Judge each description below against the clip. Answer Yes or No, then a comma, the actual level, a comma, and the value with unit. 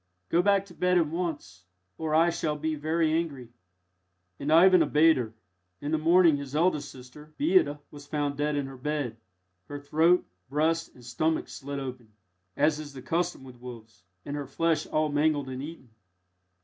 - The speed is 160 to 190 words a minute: Yes, average, 175 wpm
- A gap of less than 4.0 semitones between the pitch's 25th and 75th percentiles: Yes, average, 3.2 semitones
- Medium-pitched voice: Yes, medium, 150 Hz